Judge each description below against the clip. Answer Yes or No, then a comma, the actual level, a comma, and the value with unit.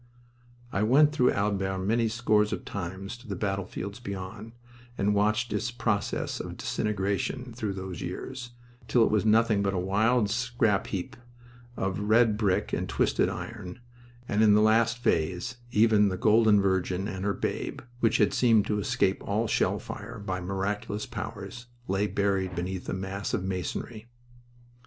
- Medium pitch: No, low, 105 Hz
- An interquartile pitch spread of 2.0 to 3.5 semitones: Yes, average, 2.7 semitones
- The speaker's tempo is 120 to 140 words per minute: No, average, 160 wpm